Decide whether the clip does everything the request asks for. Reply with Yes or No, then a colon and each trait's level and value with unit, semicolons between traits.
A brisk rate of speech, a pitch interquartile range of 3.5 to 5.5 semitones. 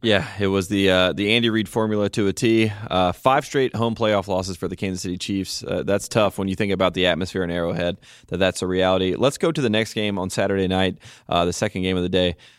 No: fast, 255 wpm; average, 2.9 semitones